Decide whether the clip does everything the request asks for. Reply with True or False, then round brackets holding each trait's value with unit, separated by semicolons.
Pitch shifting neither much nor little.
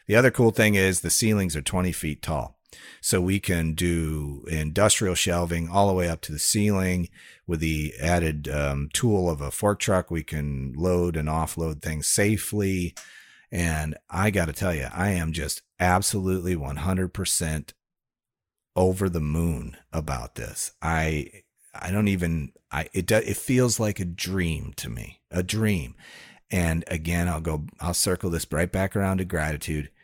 True (3.5 semitones)